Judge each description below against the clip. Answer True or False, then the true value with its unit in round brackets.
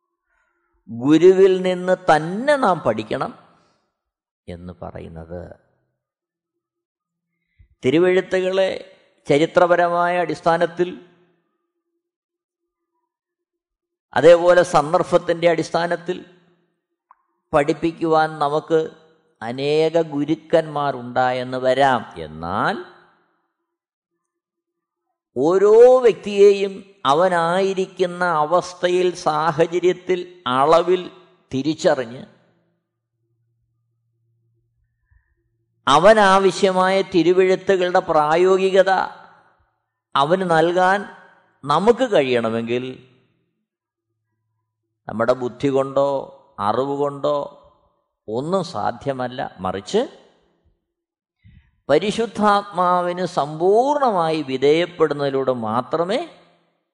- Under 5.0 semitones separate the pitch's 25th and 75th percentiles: False (5.3 semitones)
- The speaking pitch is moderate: True (170 Hz)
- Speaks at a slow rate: True (45 wpm)